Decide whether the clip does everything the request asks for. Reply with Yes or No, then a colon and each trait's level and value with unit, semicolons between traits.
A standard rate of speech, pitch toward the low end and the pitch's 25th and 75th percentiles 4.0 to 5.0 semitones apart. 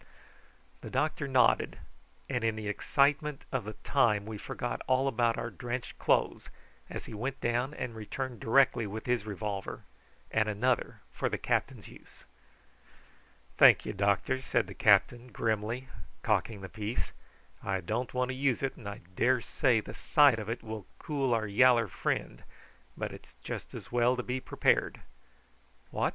No: average, 160 wpm; low, 120 Hz; average, 3.4 semitones